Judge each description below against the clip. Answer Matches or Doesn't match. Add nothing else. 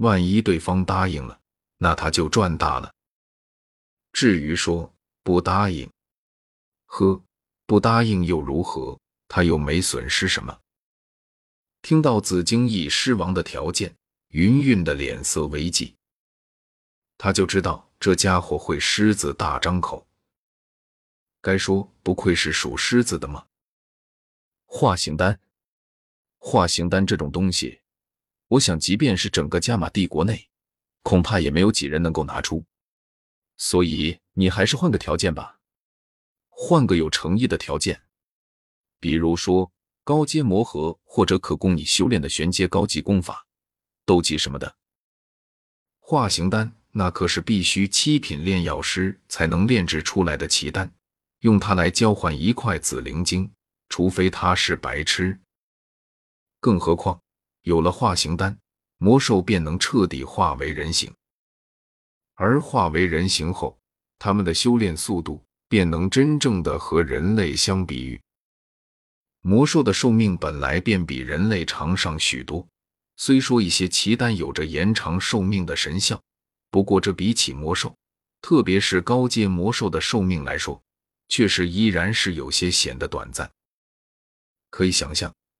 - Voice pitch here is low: Matches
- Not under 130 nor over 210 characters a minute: Matches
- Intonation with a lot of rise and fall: Doesn't match